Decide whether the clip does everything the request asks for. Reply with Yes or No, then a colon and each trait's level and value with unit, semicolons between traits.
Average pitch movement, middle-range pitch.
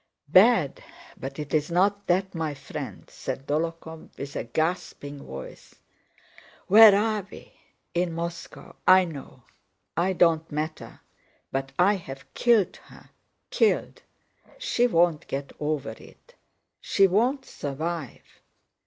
Yes: average, 5.0 semitones; medium, 170 Hz